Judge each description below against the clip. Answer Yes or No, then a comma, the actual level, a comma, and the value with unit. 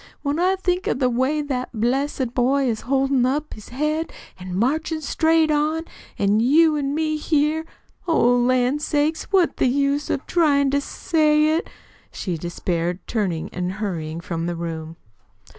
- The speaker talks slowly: No, average, 160 wpm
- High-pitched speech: Yes, very high, 275 Hz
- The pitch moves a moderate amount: No, wide, 6.0 semitones